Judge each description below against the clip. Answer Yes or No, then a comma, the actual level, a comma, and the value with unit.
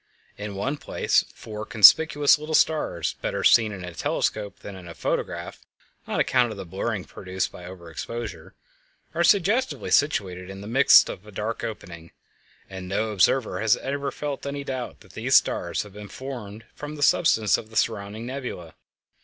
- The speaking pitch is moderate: No, low, 110 Hz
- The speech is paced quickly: No, average, 175 wpm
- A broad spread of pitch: Yes, wide, 6.1 semitones